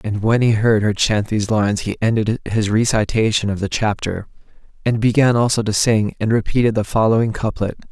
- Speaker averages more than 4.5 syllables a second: Yes, 5.5 syllables/s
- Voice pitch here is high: No, low, 110 Hz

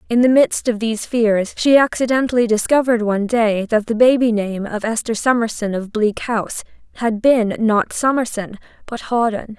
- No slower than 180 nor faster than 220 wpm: No, average, 170 wpm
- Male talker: No, female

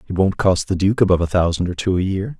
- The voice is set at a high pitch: No, very low, 95 Hz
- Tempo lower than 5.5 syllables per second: No, 6.7 syllables/s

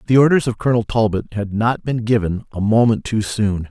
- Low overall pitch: Yes, low, 110 Hz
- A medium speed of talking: No, fast, 210 wpm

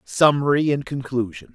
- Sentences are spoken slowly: Yes, slow, 115 wpm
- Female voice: No, male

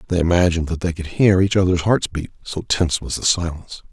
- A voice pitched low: Yes, very low, 85 Hz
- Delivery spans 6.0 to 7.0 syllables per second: Yes, 6.3 syllables/s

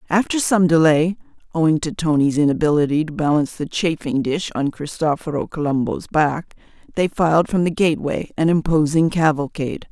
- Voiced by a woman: Yes, female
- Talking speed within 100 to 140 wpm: Yes, slow, 135 wpm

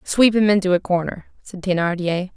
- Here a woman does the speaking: Yes, female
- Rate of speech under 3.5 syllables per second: No, 5.3 syllables/s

